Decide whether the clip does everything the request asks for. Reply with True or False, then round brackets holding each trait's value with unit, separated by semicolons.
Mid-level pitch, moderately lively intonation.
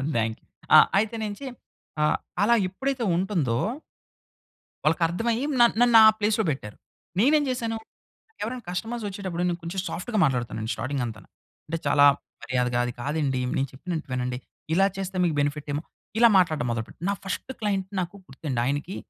False (170 Hz; 7.7 semitones)